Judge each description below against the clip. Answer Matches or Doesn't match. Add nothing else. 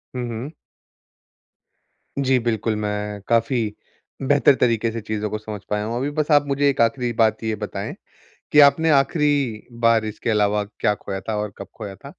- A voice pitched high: Doesn't match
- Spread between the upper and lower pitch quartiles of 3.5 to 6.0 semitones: Matches